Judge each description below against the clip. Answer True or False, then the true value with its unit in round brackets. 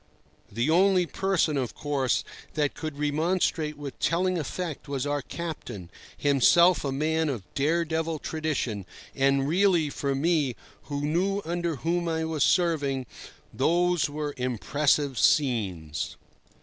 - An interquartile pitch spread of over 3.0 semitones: True (3.6 semitones)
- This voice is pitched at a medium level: True (150 Hz)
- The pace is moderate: False (130 wpm)